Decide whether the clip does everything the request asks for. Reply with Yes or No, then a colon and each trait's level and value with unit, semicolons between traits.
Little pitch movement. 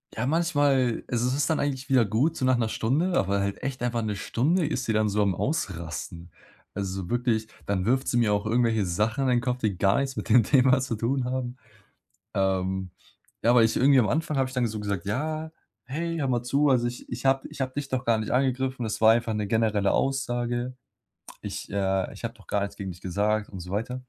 No: average, 4.3 semitones